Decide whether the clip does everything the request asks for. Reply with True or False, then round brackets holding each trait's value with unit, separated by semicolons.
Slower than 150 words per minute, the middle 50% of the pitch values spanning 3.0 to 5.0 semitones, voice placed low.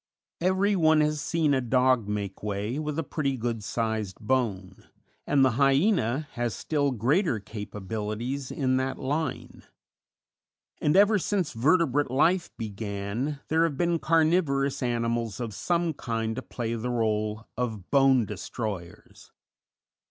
False (135 wpm; 5.4 semitones; 130 Hz)